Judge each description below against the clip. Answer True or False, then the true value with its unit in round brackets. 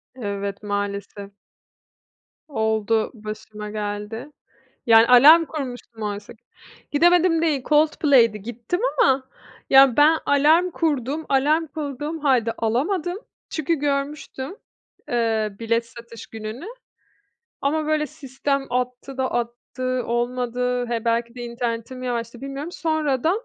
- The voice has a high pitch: True (250 Hz)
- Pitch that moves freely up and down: False (4.5 semitones)